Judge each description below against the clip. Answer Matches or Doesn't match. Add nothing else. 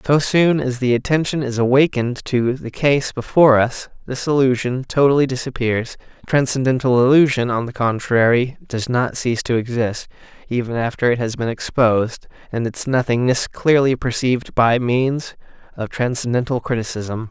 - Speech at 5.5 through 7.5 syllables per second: Doesn't match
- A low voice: Matches